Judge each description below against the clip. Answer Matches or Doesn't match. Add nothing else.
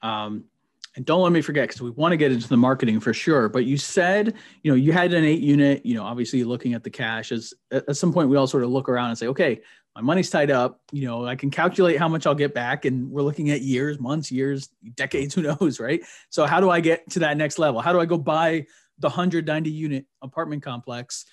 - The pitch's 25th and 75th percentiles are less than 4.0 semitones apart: Doesn't match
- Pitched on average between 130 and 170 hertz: Matches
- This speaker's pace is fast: Matches